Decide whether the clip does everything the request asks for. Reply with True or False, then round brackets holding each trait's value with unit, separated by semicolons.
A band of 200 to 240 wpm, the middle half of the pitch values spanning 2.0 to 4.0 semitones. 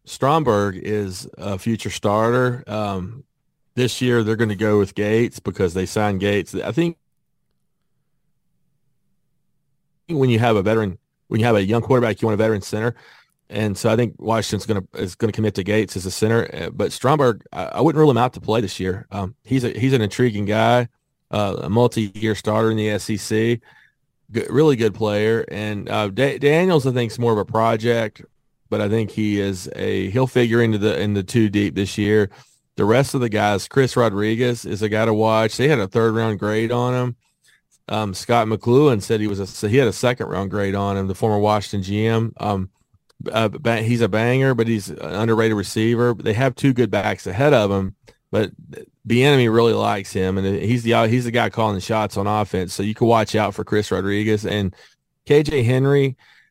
True (205 wpm; 2.8 semitones)